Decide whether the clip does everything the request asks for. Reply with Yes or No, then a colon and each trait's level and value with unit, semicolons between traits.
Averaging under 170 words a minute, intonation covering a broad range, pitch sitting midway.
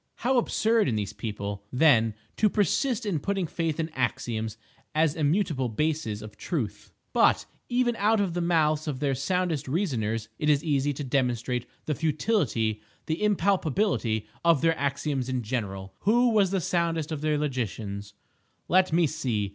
Yes: average, 160 wpm; wide, 6.8 semitones; medium, 150 Hz